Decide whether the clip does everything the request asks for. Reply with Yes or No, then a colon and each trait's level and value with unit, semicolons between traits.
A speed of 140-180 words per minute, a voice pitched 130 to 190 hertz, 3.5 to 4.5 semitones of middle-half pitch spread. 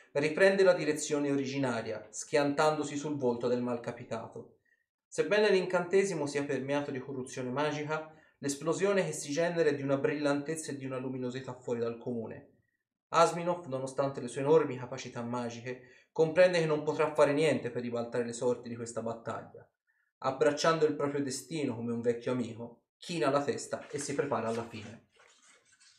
Yes: average, 155 wpm; medium, 140 Hz; average, 4.0 semitones